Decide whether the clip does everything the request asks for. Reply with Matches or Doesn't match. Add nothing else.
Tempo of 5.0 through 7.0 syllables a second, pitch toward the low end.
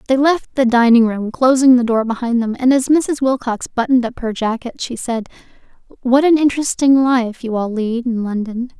Doesn't match